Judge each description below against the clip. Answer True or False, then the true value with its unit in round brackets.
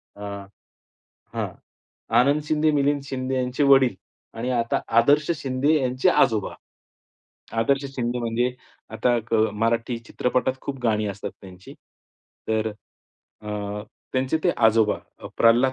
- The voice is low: True (125 Hz)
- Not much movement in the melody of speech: False (3.0 semitones)